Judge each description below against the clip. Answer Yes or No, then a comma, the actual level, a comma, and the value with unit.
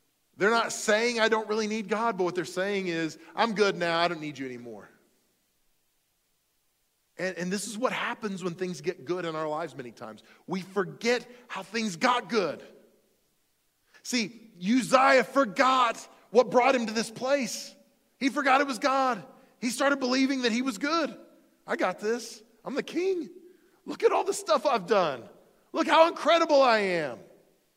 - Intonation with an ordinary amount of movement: No, wide, 6.3 semitones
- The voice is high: Yes, high, 230 Hz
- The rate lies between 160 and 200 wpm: Yes, average, 175 wpm